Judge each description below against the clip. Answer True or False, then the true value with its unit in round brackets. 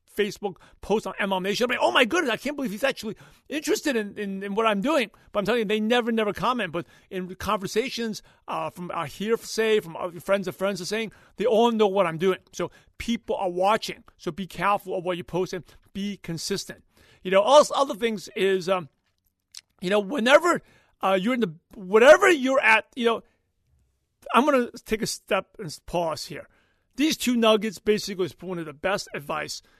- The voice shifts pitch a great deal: False (3.9 semitones)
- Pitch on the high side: True (210 Hz)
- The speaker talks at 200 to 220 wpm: True (205 wpm)